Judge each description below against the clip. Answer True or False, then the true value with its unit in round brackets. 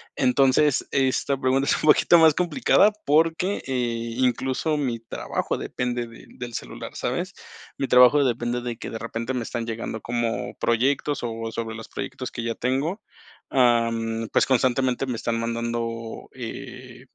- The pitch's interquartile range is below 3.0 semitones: True (2.5 semitones)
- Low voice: True (125 Hz)